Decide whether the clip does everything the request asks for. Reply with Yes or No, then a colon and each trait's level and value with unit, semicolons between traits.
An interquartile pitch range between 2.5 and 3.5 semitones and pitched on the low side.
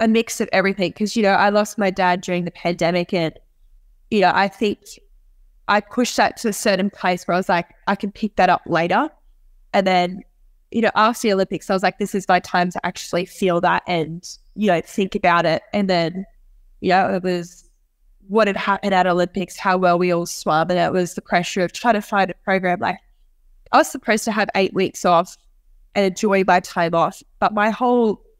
No: average, 2.8 semitones; high, 190 Hz